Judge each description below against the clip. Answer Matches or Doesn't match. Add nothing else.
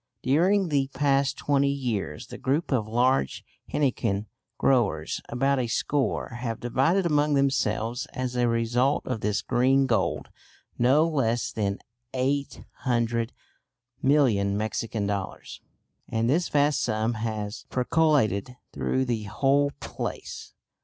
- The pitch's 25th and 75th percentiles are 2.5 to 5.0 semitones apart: Matches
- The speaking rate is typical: Doesn't match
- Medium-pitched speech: Doesn't match